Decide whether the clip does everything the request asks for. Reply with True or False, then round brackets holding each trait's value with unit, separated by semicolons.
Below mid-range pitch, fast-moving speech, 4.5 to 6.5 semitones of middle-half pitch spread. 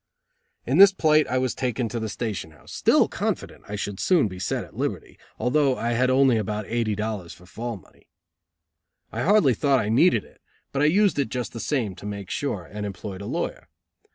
True (115 Hz; 210 wpm; 4.9 semitones)